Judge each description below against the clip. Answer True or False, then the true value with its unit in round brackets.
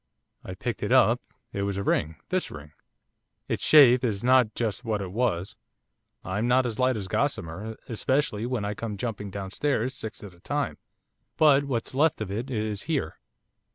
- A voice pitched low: True (110 Hz)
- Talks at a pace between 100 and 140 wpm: False (180 wpm)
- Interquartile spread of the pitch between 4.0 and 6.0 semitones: True (4.4 semitones)